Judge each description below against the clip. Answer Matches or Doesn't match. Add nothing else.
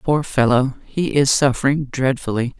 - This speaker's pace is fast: Doesn't match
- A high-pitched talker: Doesn't match